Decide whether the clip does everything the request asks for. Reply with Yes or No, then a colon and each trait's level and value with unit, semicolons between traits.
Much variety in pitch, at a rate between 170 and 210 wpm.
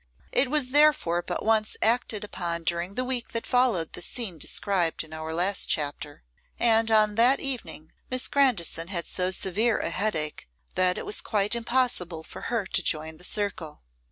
Yes: wide, 5.8 semitones; average, 175 wpm